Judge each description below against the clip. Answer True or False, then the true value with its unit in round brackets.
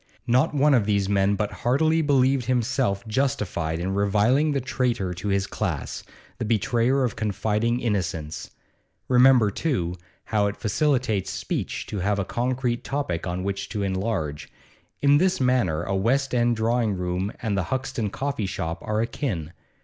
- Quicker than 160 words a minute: False (155 wpm)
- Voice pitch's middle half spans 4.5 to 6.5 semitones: True (4.8 semitones)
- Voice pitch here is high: False (110 Hz)